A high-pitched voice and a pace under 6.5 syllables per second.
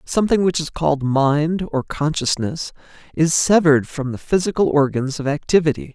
No: medium, 155 Hz; 5.2 syllables/s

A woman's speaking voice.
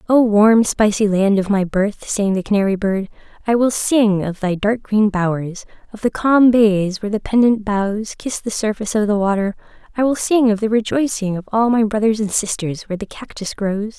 Yes: female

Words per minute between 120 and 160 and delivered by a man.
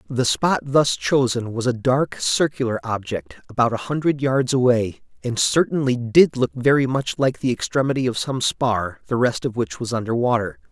No: average, 185 wpm; male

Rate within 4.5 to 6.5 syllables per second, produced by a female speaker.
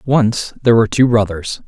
No: 5.4 syllables/s; male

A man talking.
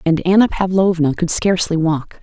No: female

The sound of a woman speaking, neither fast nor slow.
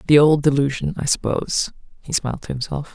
Yes: female; average, 185 wpm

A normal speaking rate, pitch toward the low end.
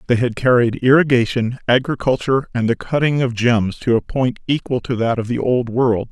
Yes: average, 195 wpm; low, 125 Hz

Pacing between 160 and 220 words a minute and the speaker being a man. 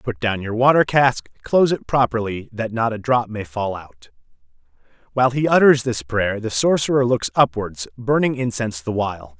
Yes: average, 180 wpm; male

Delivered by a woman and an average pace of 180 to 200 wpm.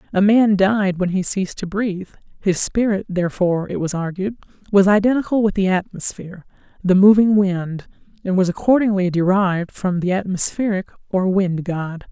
No: female; average, 150 wpm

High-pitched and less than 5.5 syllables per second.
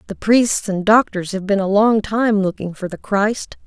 Yes: high, 205 Hz; 4.4 syllables/s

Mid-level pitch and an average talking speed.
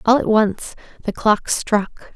No: high, 215 Hz; average, 165 wpm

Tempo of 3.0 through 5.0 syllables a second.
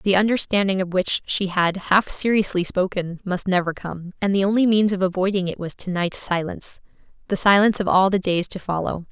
No: 5.5 syllables/s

